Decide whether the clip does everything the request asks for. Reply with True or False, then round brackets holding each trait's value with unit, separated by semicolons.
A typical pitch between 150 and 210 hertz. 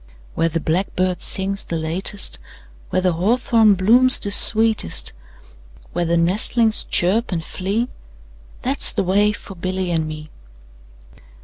True (190 Hz)